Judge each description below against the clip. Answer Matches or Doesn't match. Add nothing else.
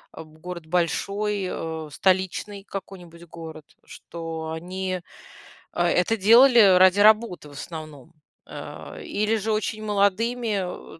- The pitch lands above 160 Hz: Matches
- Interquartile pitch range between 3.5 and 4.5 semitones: Matches